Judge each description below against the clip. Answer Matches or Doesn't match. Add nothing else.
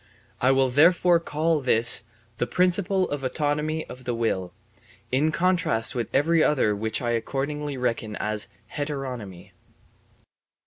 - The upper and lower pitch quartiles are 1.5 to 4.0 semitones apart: Doesn't match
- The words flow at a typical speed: Doesn't match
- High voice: Doesn't match